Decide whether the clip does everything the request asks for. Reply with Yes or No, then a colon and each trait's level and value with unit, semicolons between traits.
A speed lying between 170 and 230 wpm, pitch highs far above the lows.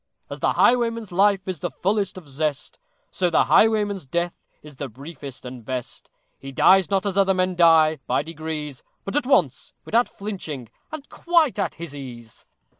Yes: average, 175 wpm; wide, 5.8 semitones